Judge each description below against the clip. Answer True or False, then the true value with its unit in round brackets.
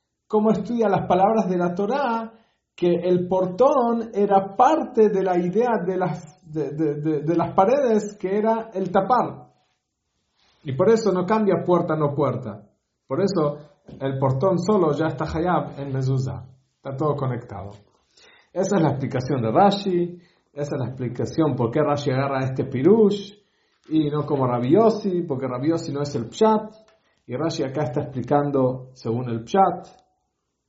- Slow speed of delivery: False (160 wpm)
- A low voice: False (170 Hz)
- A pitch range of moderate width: False (6.2 semitones)